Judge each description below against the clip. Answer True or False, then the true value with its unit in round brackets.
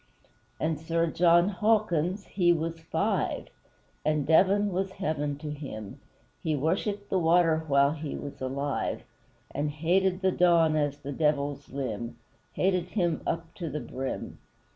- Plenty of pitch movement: False (3.6 semitones)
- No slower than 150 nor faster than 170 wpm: False (140 wpm)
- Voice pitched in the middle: True (160 Hz)